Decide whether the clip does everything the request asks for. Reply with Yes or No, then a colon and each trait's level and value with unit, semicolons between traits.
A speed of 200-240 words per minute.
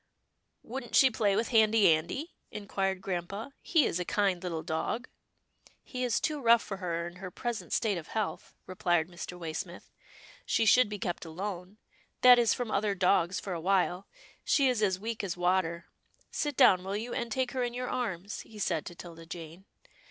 Yes: fast, 205 wpm